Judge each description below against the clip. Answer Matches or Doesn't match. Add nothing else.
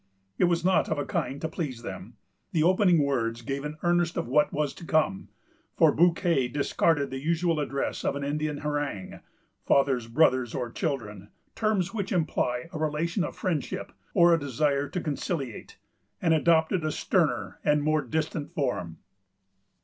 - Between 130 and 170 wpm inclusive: Matches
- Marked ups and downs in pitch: Doesn't match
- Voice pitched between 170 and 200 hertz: Doesn't match